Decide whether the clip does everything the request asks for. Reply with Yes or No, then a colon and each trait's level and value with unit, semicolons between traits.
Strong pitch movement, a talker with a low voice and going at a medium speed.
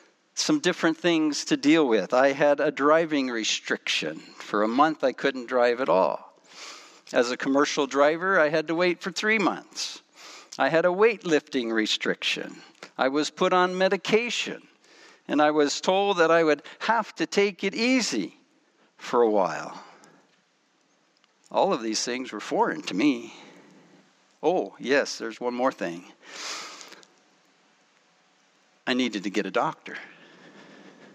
No: wide, 7.1 semitones; medium, 165 Hz; average, 145 wpm